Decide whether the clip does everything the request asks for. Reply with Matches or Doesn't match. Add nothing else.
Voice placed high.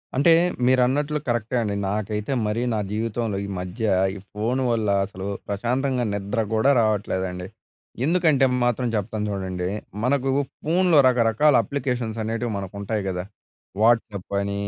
Doesn't match